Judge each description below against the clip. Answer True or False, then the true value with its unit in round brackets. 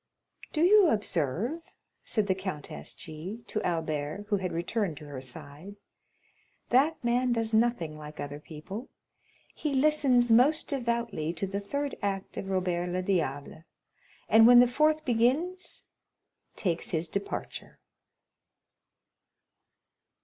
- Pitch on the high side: True (200 Hz)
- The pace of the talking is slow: True (125 wpm)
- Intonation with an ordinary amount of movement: False (7.0 semitones)